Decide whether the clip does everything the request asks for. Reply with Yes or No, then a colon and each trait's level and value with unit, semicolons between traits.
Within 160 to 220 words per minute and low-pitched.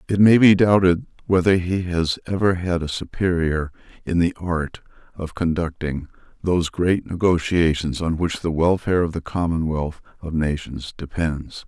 No: average, 150 wpm; very low, 85 Hz